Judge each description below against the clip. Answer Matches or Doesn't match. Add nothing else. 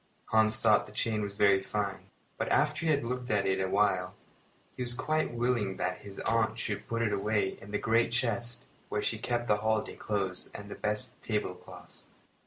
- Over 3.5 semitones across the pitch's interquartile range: Doesn't match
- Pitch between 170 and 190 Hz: Doesn't match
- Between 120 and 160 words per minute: Doesn't match